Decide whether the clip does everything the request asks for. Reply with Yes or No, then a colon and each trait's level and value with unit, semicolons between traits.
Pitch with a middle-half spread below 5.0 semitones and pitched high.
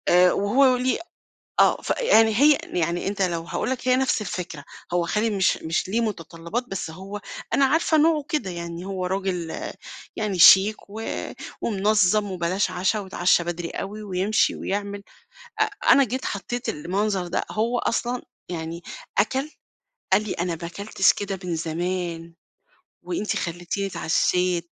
Yes: average, 3.8 semitones; high, 195 Hz